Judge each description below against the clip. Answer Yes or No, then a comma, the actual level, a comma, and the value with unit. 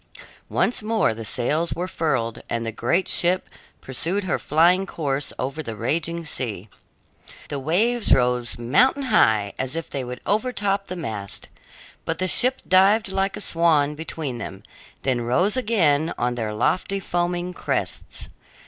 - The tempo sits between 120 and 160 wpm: Yes, average, 150 wpm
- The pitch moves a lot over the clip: Yes, wide, 7.3 semitones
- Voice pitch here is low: No, medium, 160 Hz